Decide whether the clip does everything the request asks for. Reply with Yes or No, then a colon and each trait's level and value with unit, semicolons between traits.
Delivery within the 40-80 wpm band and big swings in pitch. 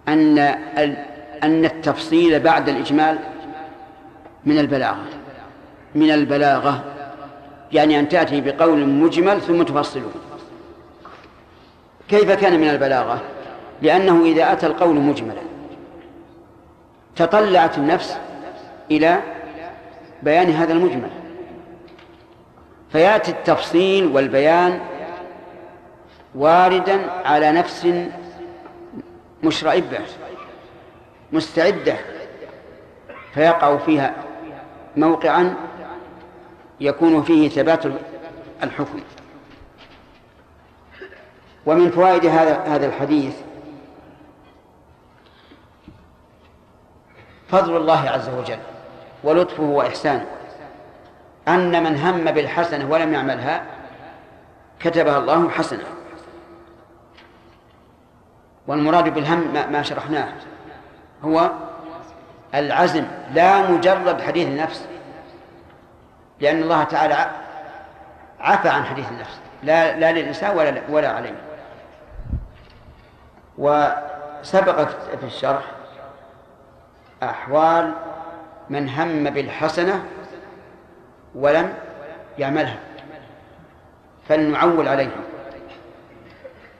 No: slow, 65 wpm; average, 2.9 semitones